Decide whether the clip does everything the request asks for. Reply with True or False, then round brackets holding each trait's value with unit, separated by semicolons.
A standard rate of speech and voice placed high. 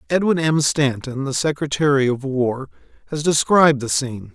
False (150 wpm; 140 Hz)